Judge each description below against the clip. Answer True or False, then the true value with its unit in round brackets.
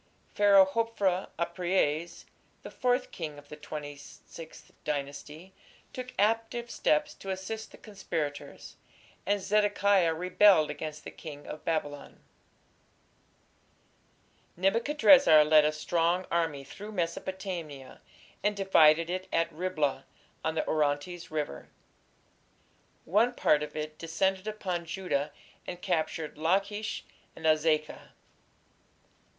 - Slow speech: True (110 wpm)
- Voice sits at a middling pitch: True (170 Hz)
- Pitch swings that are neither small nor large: True (4.5 semitones)